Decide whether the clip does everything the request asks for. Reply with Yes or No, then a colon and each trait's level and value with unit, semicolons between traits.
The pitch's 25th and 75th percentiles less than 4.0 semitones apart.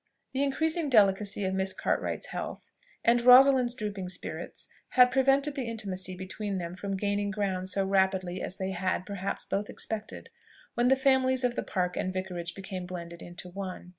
No: average, 4.8 semitones